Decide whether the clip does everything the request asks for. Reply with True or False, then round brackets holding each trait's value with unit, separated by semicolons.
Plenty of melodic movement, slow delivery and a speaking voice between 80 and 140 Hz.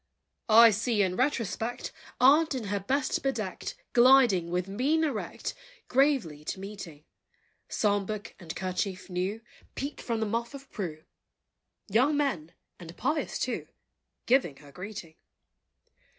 False (6.1 semitones; 130 wpm; 215 Hz)